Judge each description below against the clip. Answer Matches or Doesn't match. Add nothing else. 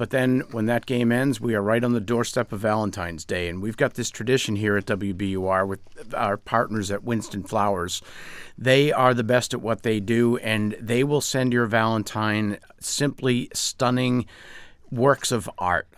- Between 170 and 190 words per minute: Matches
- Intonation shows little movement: Doesn't match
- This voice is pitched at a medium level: Doesn't match